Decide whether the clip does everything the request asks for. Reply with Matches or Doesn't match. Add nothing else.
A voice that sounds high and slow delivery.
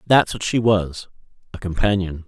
Doesn't match